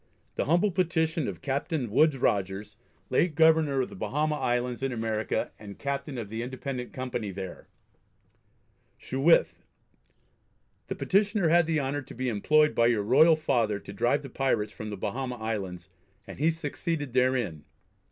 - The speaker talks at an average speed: Yes, average, 155 wpm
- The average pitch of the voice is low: Yes, low, 130 Hz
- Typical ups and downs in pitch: No, wide, 5.7 semitones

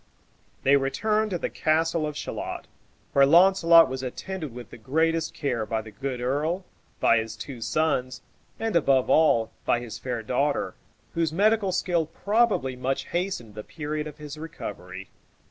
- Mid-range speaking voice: Yes, medium, 150 Hz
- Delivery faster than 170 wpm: No, average, 160 wpm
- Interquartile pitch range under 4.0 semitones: No, average, 5.0 semitones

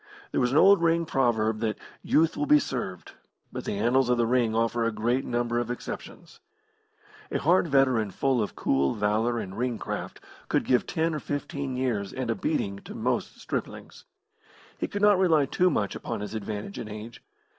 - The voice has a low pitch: Yes, low, 120 Hz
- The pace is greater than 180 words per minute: Yes, average, 190 wpm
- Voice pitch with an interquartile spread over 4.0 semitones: Yes, average, 4.6 semitones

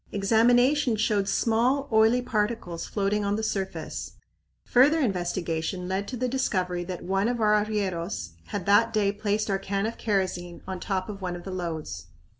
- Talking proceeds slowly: No, average, 170 wpm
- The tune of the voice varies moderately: Yes, average, 3.2 semitones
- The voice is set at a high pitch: Yes, high, 200 Hz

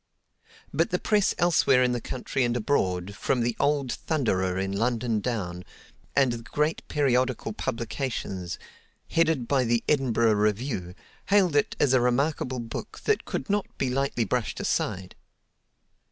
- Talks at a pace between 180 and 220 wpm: No, average, 145 wpm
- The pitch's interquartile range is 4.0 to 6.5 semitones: Yes, average, 4.3 semitones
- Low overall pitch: Yes, low, 125 Hz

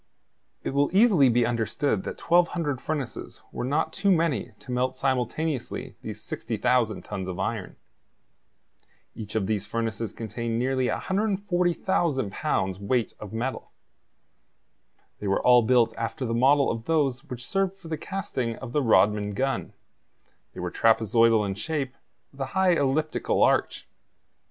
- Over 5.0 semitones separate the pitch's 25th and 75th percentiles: Yes, wide, 5.5 semitones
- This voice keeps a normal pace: Yes, average, 145 wpm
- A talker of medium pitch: No, low, 125 Hz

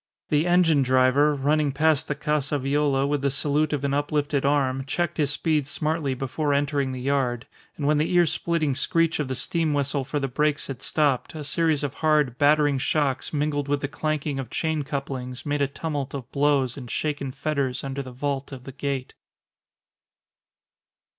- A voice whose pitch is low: No, medium, 145 Hz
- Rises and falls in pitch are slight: Yes, narrow, 1.9 semitones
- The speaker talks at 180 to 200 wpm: Yes, average, 185 wpm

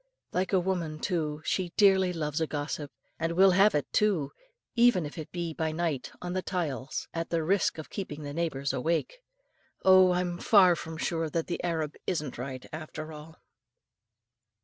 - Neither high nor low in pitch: Yes, medium, 165 Hz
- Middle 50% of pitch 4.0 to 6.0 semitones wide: No, average, 3.1 semitones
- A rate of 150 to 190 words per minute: Yes, average, 175 wpm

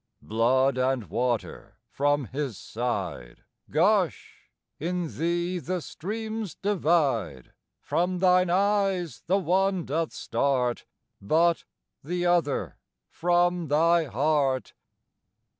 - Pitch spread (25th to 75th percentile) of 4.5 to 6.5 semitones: Yes, average, 5.2 semitones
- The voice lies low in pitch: No, medium, 165 Hz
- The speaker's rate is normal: No, slow, 95 wpm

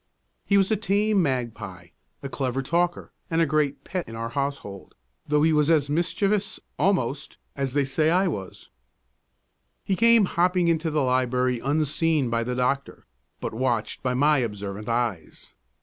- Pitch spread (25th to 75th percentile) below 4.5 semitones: No, average, 5.3 semitones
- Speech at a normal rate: Yes, average, 160 wpm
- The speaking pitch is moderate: Yes, medium, 145 Hz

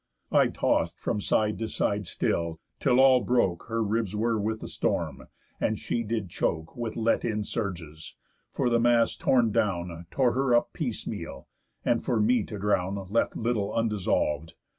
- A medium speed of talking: Yes, average, 165 wpm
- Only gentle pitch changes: No, average, 3.5 semitones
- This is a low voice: Yes, low, 110 Hz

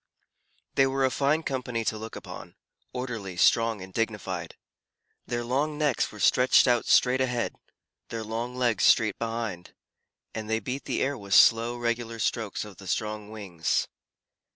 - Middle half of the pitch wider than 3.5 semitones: No, average, 2.9 semitones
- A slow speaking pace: No, average, 155 wpm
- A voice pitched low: Yes, low, 115 Hz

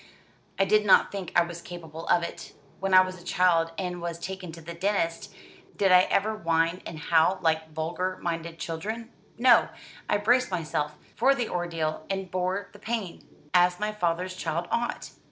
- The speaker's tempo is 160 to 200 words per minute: Yes, average, 180 wpm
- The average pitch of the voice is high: No, medium, 180 Hz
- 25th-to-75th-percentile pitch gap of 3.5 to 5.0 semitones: No, average, 2.7 semitones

